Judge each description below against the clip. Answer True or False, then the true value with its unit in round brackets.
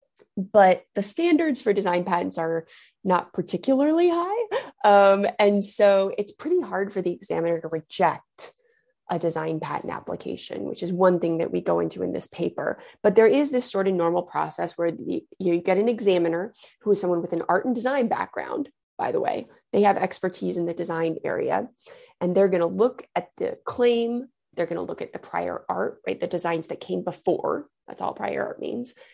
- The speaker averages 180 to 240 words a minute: True (200 wpm)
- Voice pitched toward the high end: True (195 Hz)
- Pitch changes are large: True (6.3 semitones)